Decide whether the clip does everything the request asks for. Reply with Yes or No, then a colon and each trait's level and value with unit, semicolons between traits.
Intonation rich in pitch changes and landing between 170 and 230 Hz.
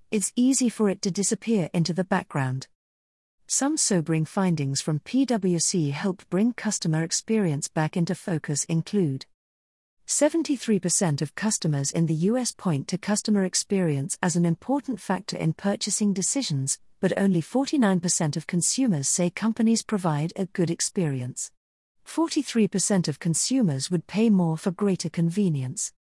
No: average, 4.9 semitones; medium, 185 Hz